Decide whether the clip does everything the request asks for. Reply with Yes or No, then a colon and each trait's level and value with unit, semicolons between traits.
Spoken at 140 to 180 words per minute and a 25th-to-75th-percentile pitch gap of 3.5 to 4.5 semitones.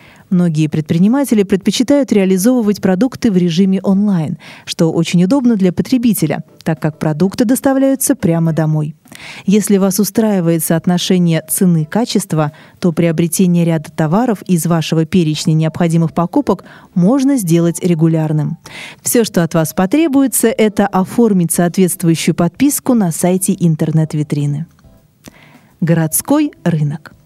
No: slow, 110 wpm; average, 4.2 semitones